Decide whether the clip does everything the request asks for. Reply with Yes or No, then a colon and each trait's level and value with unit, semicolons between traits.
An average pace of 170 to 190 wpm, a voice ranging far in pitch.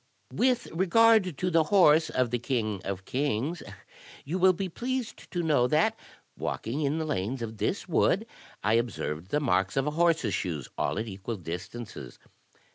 Yes: average, 175 wpm; wide, 7.9 semitones